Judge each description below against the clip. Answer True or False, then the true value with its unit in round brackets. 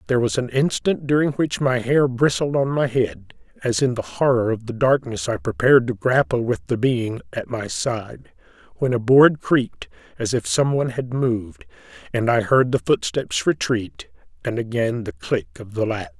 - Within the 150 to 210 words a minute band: True (190 wpm)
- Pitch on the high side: False (125 Hz)